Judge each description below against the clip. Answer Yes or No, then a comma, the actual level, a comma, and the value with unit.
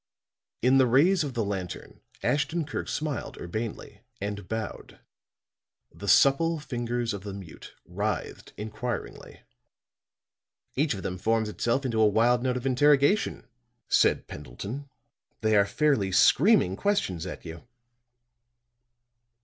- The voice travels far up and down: Yes, wide, 5.7 semitones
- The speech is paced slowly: Yes, slow, 125 wpm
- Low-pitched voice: Yes, low, 120 Hz